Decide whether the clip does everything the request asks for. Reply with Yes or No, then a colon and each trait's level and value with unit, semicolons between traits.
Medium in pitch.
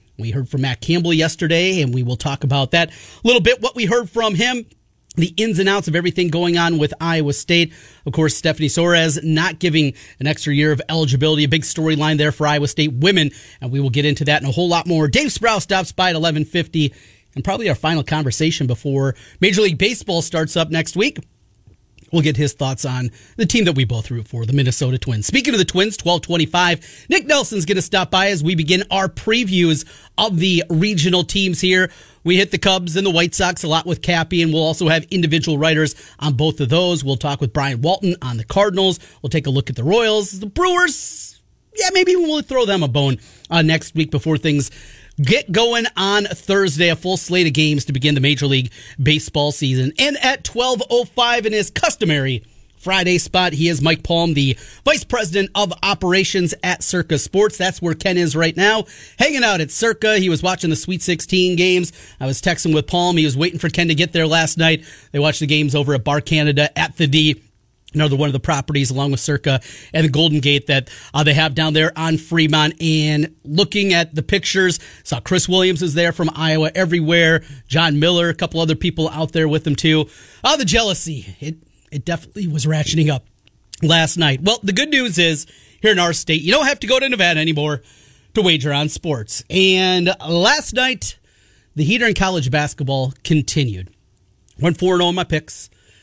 Yes: medium, 160 Hz